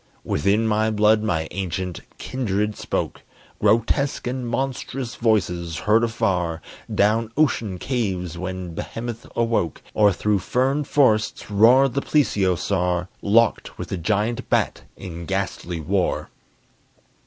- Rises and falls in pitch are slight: No, average, 4.3 semitones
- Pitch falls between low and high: No, low, 105 Hz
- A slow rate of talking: Yes, slow, 120 wpm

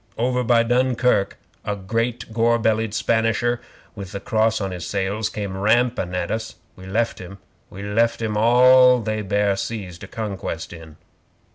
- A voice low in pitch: Yes, low, 110 Hz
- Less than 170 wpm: Yes, average, 160 wpm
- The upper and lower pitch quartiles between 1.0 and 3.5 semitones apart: Yes, average, 3.1 semitones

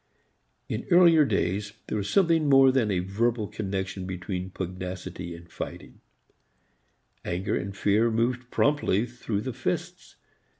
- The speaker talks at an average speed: No, slow, 130 wpm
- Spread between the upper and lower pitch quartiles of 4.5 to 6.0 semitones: Yes, average, 5.1 semitones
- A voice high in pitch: No, low, 105 Hz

